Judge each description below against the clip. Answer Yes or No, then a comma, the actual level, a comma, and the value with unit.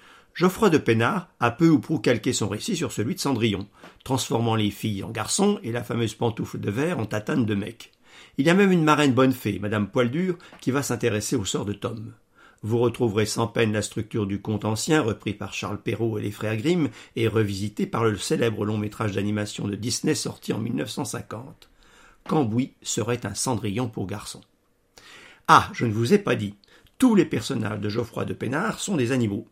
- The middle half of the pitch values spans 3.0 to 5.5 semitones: Yes, average, 3.8 semitones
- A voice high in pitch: No, low, 115 Hz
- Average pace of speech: Yes, average, 200 wpm